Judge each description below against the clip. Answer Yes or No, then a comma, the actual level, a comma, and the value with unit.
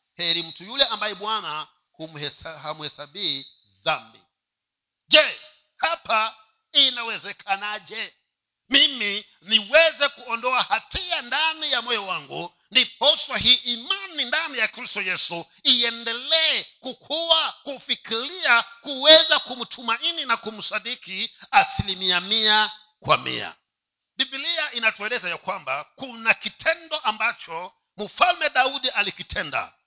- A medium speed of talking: No, slow, 95 wpm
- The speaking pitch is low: No, high, 235 Hz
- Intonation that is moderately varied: No, wide, 5.9 semitones